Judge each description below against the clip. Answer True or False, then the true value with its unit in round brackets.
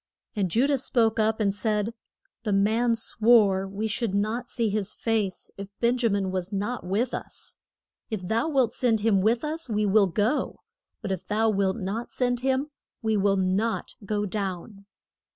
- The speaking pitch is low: False (215 Hz)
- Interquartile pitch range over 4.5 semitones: False (2.9 semitones)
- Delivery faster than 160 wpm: True (180 wpm)